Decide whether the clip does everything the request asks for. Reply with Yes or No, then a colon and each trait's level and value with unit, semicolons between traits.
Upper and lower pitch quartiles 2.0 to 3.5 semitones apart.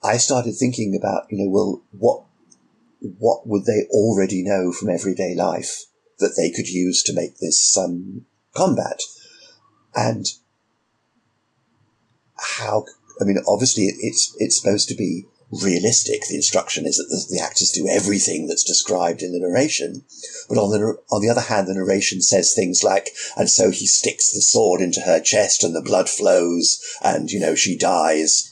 No: average, 3.9 semitones